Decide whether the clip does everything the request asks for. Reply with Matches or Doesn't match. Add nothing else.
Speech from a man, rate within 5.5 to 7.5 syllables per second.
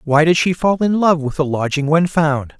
Doesn't match